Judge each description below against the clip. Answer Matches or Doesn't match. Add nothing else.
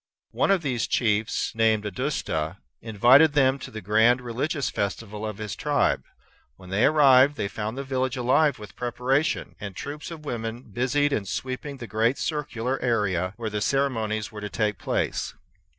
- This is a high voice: Doesn't match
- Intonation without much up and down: Doesn't match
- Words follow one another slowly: Doesn't match